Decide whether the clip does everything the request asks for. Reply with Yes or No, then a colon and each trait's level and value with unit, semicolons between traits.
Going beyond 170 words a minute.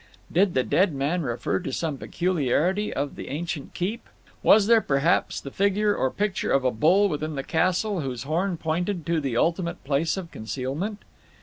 Yes: average, 180 wpm